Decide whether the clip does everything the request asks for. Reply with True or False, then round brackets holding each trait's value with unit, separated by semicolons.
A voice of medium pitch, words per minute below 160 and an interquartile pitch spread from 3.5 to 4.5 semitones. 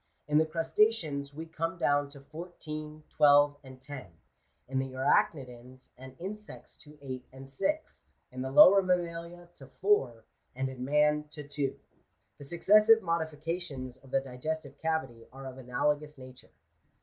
True (145 Hz; 150 wpm; 3.8 semitones)